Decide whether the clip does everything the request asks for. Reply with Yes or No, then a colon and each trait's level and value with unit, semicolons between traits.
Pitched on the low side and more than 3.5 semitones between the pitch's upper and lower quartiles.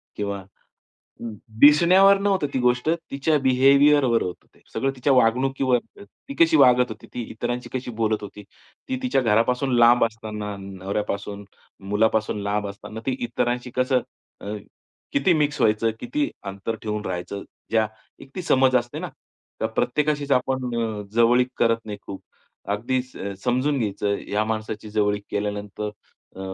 Yes: low, 120 Hz; average, 4.1 semitones